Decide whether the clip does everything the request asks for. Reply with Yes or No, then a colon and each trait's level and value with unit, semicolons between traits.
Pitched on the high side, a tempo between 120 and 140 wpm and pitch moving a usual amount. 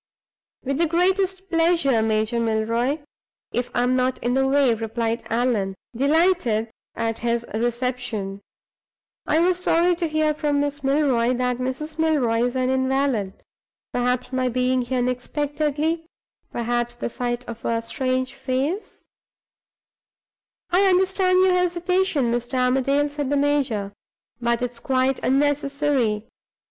Yes: very high, 260 Hz; slow, 135 wpm; average, 4.0 semitones